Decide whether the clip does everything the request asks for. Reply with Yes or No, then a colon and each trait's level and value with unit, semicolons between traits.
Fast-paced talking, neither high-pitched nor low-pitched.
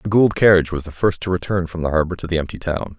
No: fast, 300 wpm; very low, 85 Hz